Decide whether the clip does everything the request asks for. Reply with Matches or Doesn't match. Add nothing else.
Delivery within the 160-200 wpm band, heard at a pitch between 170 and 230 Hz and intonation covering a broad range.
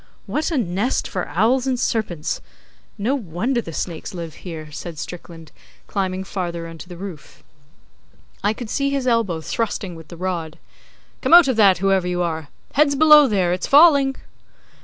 Matches